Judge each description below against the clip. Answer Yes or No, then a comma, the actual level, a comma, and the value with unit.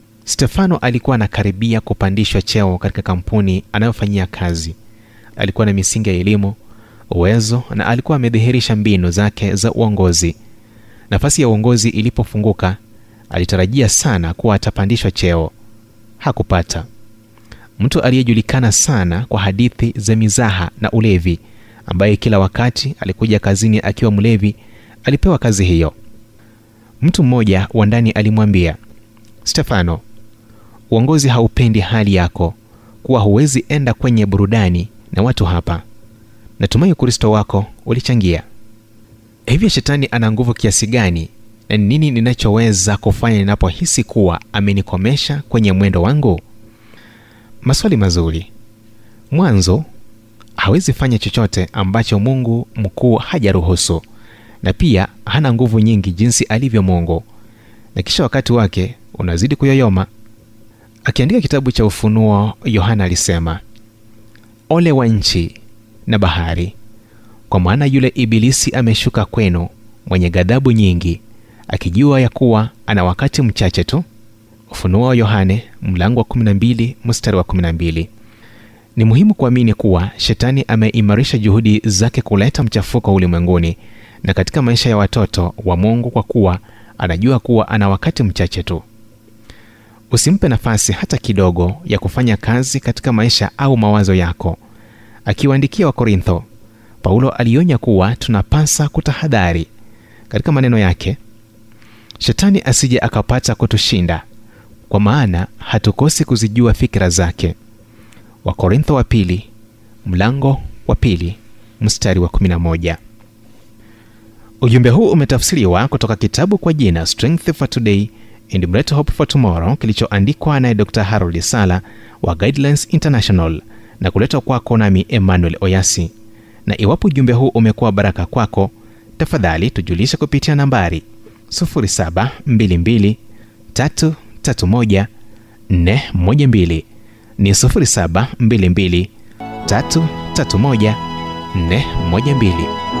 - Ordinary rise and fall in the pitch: Yes, average, 3.0 semitones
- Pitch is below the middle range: Yes, low, 110 Hz